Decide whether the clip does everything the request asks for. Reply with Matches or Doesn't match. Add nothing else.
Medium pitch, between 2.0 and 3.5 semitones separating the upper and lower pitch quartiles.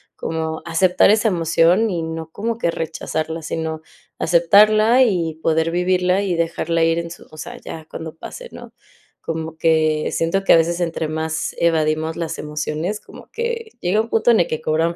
Matches